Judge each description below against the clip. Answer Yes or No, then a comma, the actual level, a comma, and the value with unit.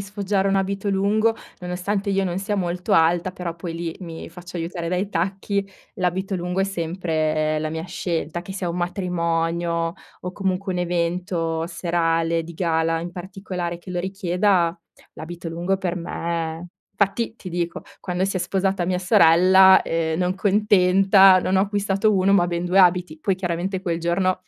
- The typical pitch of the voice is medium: Yes, medium, 180 Hz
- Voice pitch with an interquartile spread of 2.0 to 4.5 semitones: Yes, narrow, 2.3 semitones